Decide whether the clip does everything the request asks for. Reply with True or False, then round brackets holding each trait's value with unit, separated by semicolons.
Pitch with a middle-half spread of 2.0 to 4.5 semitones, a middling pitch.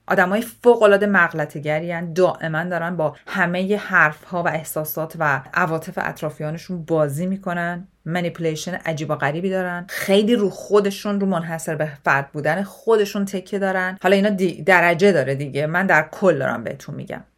True (3.5 semitones; 175 Hz)